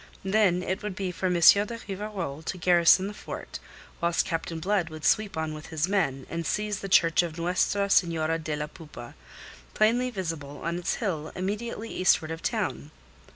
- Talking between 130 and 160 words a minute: No, average, 185 wpm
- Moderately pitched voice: Yes, medium, 175 Hz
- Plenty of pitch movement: No, average, 3.7 semitones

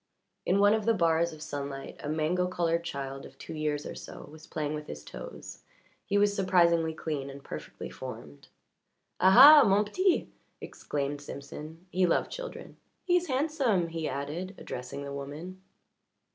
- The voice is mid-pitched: Yes, medium, 165 Hz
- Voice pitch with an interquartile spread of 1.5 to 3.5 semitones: No, average, 5.2 semitones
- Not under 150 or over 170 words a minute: Yes, average, 160 wpm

